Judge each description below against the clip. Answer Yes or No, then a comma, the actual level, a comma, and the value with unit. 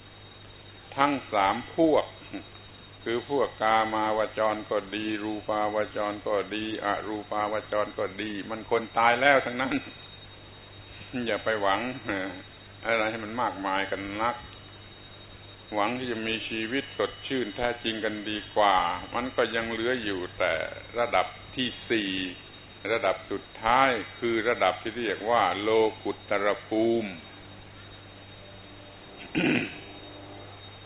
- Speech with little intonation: Yes, narrow, 2.0 semitones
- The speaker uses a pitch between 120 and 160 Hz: No, low, 105 Hz